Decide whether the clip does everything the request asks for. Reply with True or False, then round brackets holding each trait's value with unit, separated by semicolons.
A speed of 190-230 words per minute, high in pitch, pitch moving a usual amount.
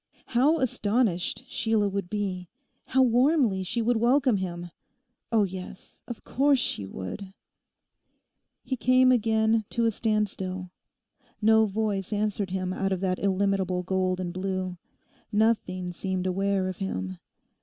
False (135 wpm; 200 Hz; 3.4 semitones)